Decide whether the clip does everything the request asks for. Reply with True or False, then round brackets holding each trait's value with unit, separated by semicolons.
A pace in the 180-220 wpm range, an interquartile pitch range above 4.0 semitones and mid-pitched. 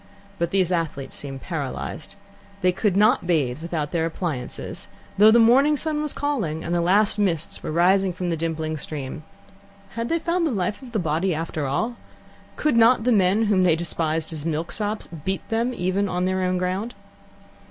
True (185 wpm; 5.1 semitones; 180 Hz)